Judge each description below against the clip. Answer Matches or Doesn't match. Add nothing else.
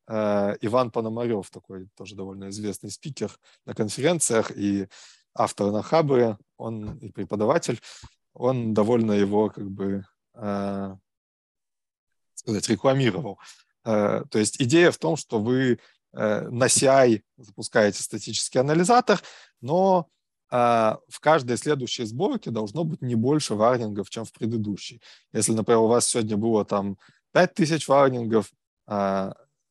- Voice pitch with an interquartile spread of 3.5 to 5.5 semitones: Matches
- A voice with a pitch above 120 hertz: Doesn't match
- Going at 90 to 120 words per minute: Matches